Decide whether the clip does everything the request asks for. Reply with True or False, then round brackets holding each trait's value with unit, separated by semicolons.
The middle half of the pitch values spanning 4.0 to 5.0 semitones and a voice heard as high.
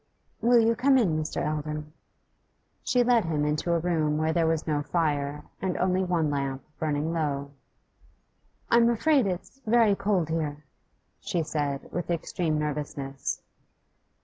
False (4.3 semitones; 160 Hz)